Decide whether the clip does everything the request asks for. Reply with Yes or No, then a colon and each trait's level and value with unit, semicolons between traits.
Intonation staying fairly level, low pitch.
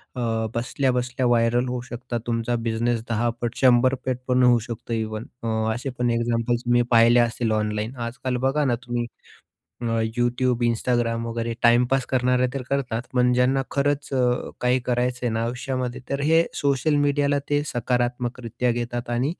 Yes: narrow, 1.5 semitones; low, 125 Hz